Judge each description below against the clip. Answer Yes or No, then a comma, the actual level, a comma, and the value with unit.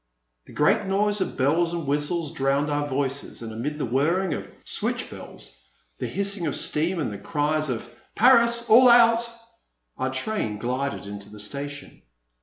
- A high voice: No, medium, 150 Hz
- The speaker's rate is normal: Yes, average, 170 wpm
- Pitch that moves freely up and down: Yes, wide, 6.3 semitones